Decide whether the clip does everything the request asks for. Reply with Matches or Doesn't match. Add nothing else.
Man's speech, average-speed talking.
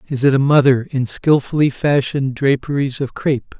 Matches